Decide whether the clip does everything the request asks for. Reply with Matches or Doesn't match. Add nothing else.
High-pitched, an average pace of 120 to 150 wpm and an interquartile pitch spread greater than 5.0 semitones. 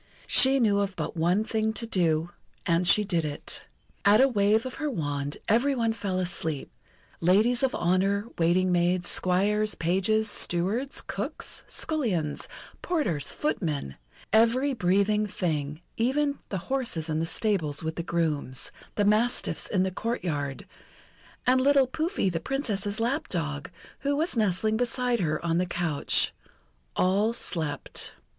Matches